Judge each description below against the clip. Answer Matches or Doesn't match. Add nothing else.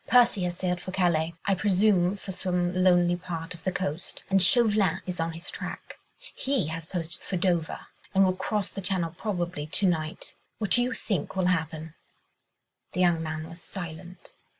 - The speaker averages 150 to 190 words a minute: Matches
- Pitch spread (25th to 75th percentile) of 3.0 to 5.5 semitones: Doesn't match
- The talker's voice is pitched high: Doesn't match